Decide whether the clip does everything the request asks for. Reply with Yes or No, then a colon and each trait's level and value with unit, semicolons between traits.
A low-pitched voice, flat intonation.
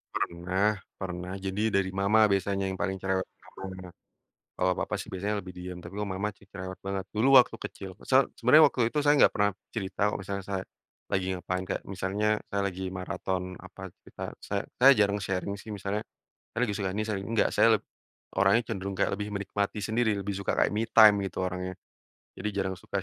Yes: low, 100 Hz; narrow, 1.9 semitones